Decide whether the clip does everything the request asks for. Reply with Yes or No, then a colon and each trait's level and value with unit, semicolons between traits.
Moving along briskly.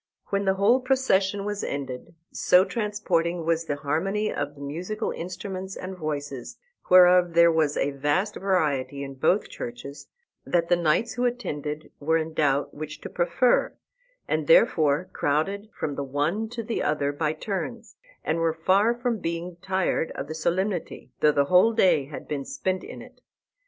No: average, 165 wpm